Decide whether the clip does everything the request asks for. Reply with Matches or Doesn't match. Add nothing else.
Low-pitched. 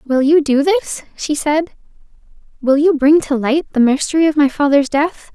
Doesn't match